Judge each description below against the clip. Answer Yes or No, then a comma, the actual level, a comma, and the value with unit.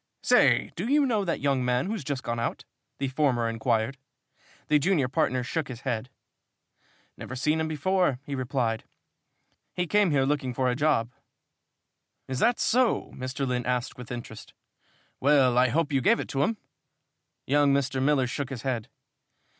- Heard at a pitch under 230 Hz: Yes, low, 135 Hz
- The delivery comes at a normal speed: Yes, average, 170 wpm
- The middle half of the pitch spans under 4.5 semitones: Yes, average, 3.4 semitones